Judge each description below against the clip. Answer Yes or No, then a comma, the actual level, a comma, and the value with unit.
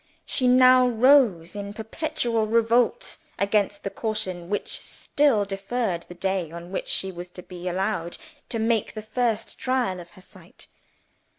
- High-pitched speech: Yes, high, 210 Hz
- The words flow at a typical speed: Yes, average, 155 wpm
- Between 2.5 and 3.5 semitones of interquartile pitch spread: No, average, 4.4 semitones